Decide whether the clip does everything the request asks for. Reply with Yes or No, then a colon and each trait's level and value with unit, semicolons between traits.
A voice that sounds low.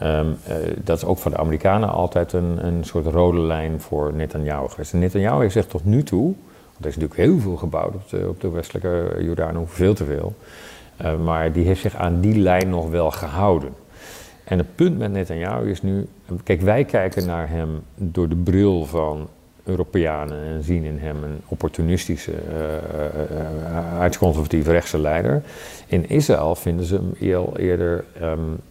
Yes: very low, 85 Hz